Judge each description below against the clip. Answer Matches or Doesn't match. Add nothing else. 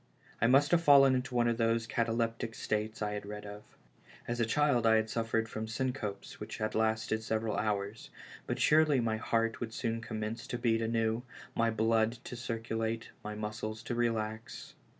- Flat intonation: Matches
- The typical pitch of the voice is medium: Doesn't match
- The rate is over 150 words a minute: Matches